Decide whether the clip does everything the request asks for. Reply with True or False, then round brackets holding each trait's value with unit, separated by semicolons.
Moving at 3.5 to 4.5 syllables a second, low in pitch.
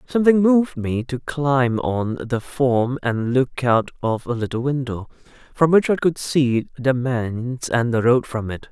True (4.2 syllables/s; 130 Hz)